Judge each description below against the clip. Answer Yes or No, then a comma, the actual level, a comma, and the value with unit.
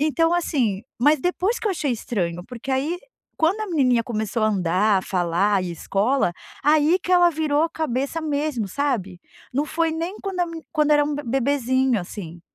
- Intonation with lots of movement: Yes, wide, 6.9 semitones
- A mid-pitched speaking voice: No, very high, 275 Hz